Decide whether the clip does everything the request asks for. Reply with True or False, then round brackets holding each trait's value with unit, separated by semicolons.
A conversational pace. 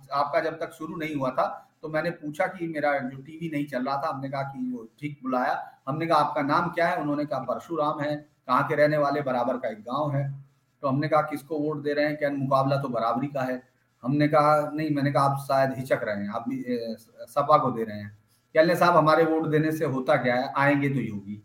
False (245 wpm)